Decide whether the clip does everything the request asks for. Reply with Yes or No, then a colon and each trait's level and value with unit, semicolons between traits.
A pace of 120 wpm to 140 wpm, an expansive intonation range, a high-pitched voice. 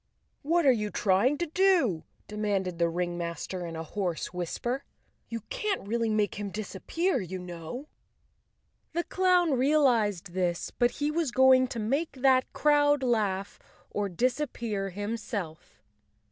Yes: slow, 135 wpm; wide, 6.8 semitones; high, 220 Hz